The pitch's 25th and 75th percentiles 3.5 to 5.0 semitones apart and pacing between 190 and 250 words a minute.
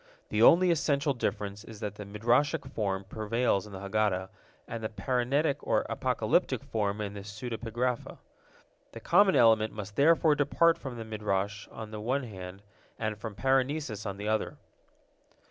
No: average, 4.0 semitones; average, 160 wpm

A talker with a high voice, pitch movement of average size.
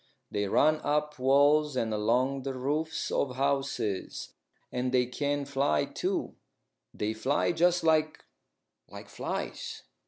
No: medium, 140 Hz; average, 3.2 semitones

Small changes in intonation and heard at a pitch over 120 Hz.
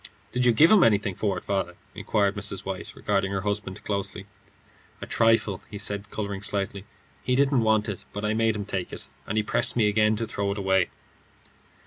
No: narrow, 1.8 semitones; low, 105 Hz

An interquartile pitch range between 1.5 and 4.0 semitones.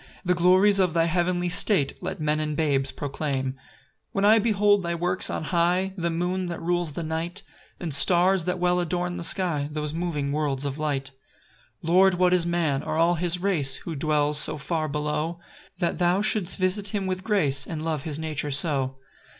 Yes: average, 3.3 semitones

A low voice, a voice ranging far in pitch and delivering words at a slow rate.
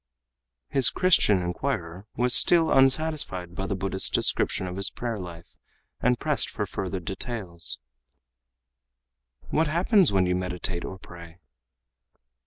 Yes: very low, 95 Hz; wide, 6.9 semitones; slow, 125 wpm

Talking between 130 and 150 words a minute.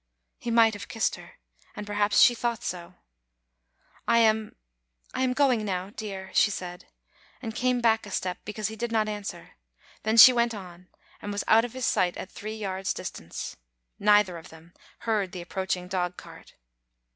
No: average, 180 wpm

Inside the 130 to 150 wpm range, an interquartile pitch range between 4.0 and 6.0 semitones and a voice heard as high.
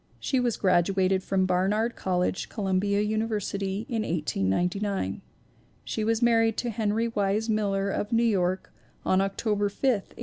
No: average, 145 wpm; average, 2.8 semitones; high, 205 Hz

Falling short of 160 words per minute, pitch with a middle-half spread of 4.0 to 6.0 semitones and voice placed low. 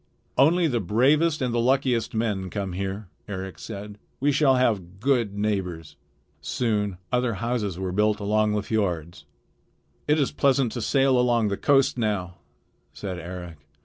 Yes: average, 150 wpm; average, 4.8 semitones; low, 105 Hz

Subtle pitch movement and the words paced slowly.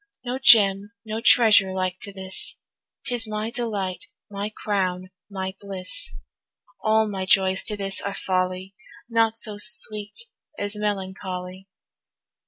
Yes: narrow, 2.3 semitones; slow, 125 wpm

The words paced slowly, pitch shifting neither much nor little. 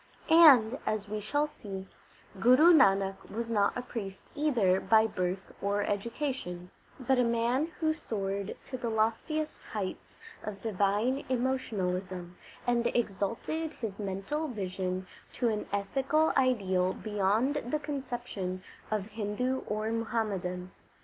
Yes: slow, 125 wpm; average, 4.7 semitones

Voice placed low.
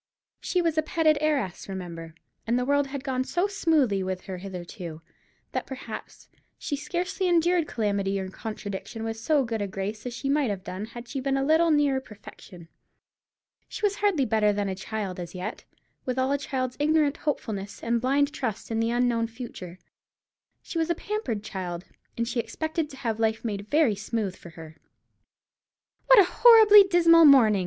No: high, 240 Hz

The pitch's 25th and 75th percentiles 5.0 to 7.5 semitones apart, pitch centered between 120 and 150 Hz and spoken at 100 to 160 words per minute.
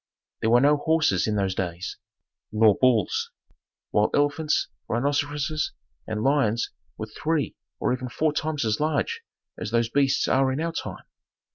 Yes: average, 5.3 semitones; low, 135 Hz; average, 150 wpm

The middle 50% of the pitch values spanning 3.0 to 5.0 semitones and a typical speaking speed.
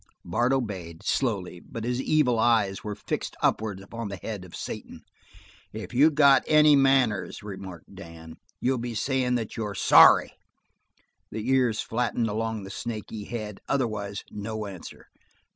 Yes: average, 3.8 semitones; average, 145 wpm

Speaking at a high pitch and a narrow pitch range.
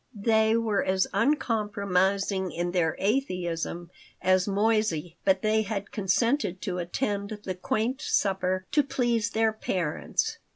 No: high, 200 Hz; average, 3.1 semitones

